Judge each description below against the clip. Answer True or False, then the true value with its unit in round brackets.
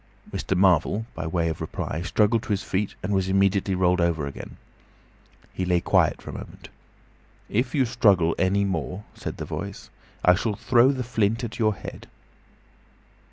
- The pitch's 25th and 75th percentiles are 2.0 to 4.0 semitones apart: True (3.4 semitones)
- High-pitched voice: False (95 Hz)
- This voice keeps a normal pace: True (170 wpm)